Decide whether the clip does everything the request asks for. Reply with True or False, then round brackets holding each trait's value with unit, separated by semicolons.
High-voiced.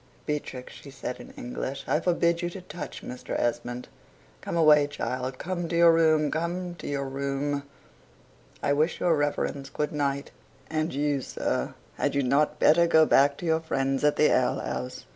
False (145 Hz)